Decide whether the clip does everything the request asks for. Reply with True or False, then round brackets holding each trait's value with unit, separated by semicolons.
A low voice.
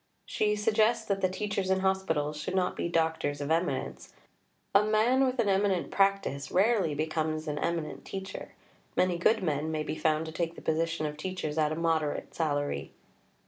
False (170 Hz)